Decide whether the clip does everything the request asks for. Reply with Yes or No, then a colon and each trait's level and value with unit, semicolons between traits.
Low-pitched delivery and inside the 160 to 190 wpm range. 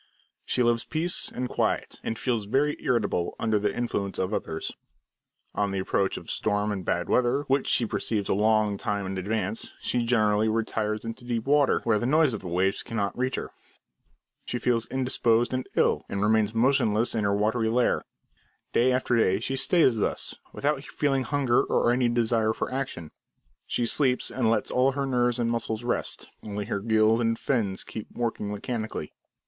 Yes: low, 115 Hz; average, 180 wpm